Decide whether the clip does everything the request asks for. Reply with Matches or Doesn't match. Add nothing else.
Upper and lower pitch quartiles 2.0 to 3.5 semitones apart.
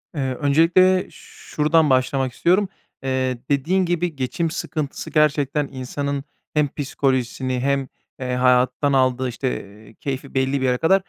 Matches